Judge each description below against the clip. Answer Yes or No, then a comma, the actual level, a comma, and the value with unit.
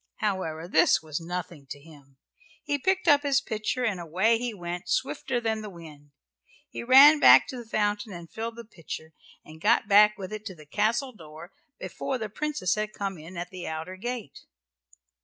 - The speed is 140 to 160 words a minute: No, average, 190 wpm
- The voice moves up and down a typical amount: No, wide, 5.8 semitones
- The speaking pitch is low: No, high, 200 Hz